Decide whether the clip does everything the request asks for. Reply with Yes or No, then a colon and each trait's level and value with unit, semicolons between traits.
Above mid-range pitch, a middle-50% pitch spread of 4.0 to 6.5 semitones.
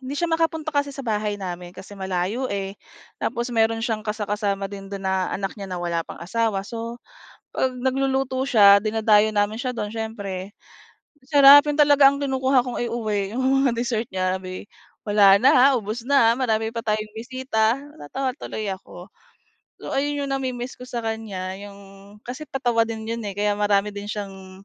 Yes: high, 220 Hz; average, 4.3 semitones